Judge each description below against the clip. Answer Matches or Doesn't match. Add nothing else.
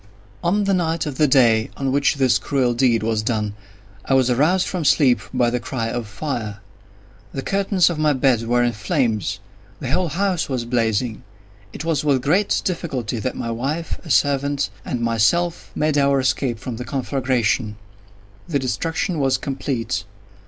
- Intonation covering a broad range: Doesn't match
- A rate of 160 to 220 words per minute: Matches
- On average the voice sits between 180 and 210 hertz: Doesn't match